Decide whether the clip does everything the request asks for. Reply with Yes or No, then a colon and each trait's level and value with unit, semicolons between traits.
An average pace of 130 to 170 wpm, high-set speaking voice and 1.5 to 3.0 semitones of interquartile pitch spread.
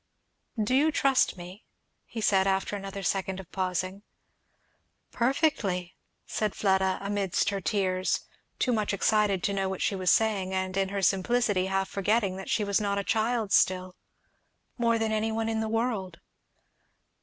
Yes: average, 160 wpm; high, 200 Hz; narrow, 2.6 semitones